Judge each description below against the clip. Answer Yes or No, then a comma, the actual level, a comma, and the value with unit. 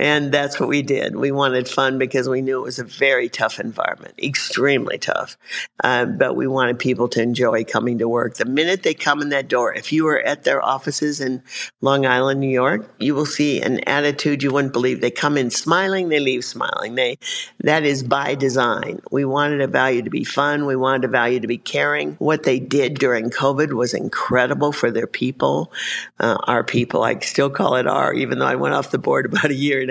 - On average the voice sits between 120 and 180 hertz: Yes, low, 135 Hz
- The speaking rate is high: Yes, fast, 220 wpm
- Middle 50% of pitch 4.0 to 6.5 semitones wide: No, narrow, 2.5 semitones